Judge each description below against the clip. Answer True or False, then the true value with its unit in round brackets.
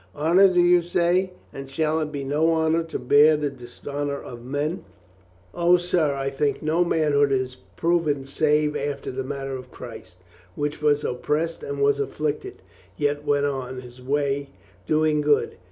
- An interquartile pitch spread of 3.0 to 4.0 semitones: False (2.5 semitones)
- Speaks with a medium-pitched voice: True (145 Hz)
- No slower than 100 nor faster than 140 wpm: False (175 wpm)